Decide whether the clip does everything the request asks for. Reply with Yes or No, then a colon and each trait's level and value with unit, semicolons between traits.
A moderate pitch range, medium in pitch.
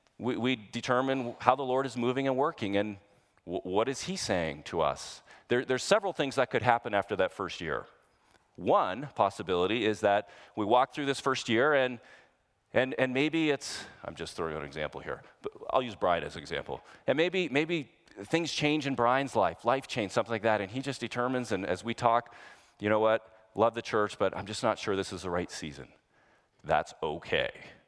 No: average, 4.0 semitones; low, 125 Hz